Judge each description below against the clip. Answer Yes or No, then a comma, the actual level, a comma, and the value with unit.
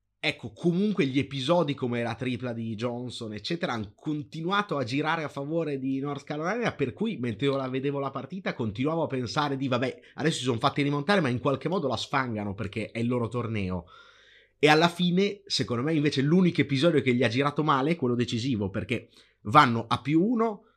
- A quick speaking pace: Yes, fast, 195 wpm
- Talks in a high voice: No, medium, 140 Hz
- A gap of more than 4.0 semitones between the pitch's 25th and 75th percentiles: Yes, average, 4.6 semitones